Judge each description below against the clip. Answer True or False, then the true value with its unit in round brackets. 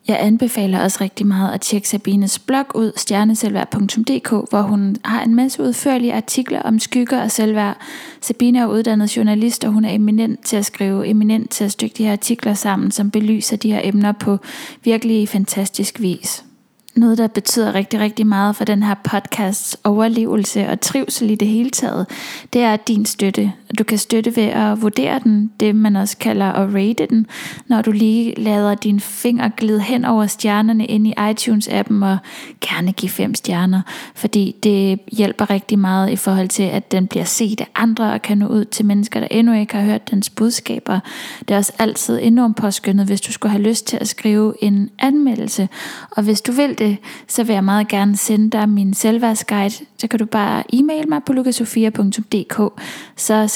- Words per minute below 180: False (190 wpm)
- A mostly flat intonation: True (2.1 semitones)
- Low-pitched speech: False (215 Hz)